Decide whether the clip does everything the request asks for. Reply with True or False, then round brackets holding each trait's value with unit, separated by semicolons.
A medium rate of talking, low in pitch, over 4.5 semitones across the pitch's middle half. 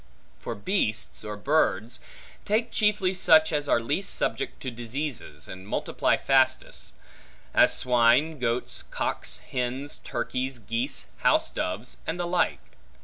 False (130 wpm; 130 Hz; 5.2 semitones)